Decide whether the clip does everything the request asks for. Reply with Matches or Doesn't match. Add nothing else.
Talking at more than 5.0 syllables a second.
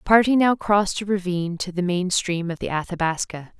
Matches